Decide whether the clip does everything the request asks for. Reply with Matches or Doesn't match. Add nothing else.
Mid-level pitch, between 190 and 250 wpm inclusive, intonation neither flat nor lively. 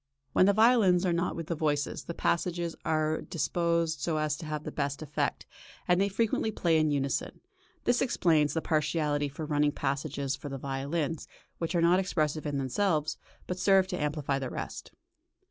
Doesn't match